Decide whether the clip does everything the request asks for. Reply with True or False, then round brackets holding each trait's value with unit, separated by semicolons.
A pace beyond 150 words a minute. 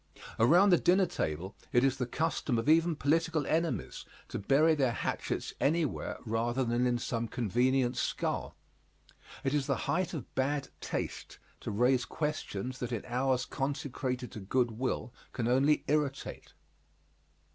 False (145 wpm)